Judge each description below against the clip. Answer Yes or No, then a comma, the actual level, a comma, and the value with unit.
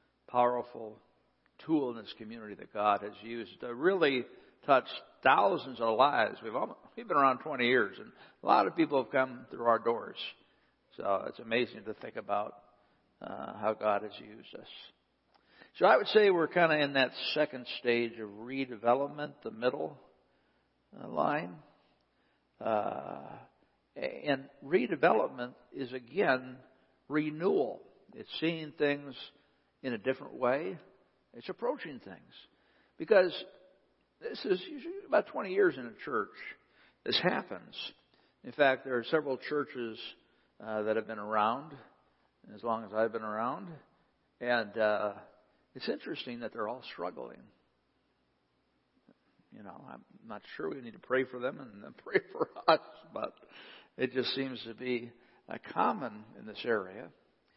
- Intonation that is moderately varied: Yes, average, 3.7 semitones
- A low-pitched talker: Yes, low, 125 Hz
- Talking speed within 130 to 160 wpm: Yes, average, 145 wpm